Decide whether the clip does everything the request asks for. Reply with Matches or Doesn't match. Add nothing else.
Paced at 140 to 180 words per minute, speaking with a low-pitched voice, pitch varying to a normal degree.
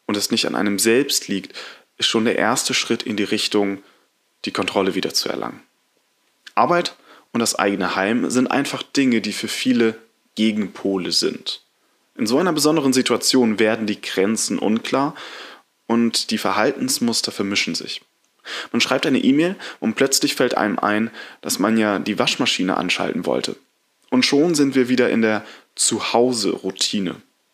Matches